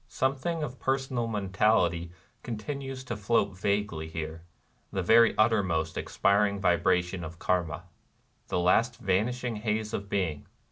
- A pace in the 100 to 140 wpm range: Yes, slow, 135 wpm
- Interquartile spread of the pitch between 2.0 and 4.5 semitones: No, average, 4.9 semitones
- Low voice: Yes, low, 100 Hz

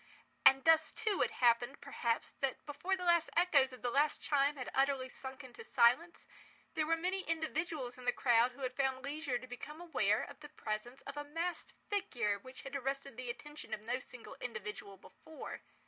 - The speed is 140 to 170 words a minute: No, average, 195 wpm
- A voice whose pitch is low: No, very high, 275 Hz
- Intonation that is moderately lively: Yes, average, 4.1 semitones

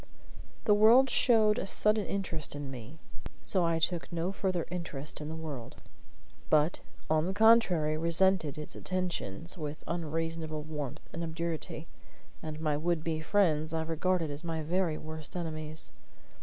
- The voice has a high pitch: No, medium, 165 Hz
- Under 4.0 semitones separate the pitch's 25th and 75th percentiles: Yes, average, 2.9 semitones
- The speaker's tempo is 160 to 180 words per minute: No, average, 150 wpm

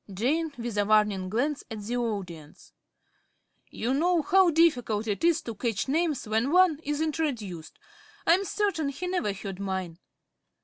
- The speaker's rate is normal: Yes, average, 160 wpm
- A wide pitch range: Yes, wide, 7.8 semitones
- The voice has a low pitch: No, high, 245 Hz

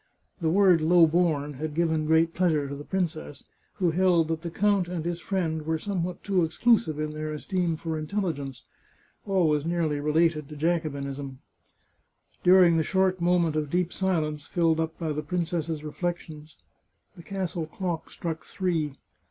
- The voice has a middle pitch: Yes, medium, 165 Hz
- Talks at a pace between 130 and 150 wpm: No, average, 170 wpm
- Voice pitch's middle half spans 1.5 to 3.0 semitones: Yes, narrow, 2.6 semitones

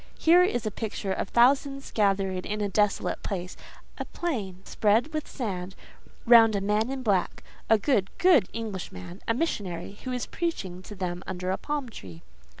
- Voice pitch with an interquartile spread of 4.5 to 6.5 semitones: Yes, average, 5.0 semitones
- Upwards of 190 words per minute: No, average, 150 wpm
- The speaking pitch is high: Yes, high, 210 Hz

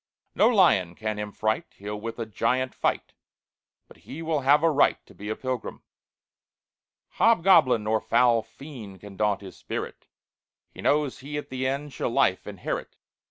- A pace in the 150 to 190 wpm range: Yes, average, 165 wpm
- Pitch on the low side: Yes, low, 125 Hz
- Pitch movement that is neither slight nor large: No, wide, 5.7 semitones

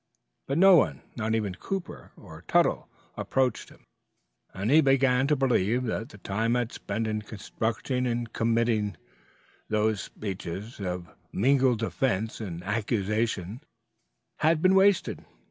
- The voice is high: No, low, 115 Hz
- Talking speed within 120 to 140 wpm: Yes, slow, 135 wpm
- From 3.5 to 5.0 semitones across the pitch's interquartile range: Yes, average, 4.1 semitones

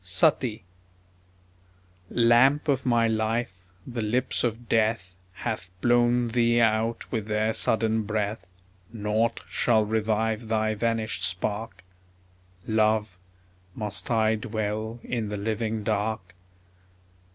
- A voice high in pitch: No, low, 110 Hz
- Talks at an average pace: No, slow, 105 wpm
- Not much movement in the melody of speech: Yes, narrow, 1.6 semitones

